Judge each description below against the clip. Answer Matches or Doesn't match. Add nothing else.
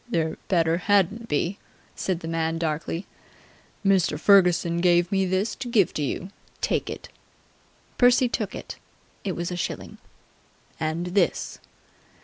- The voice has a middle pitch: Matches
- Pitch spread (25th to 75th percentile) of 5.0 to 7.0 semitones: Doesn't match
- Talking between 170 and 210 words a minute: Doesn't match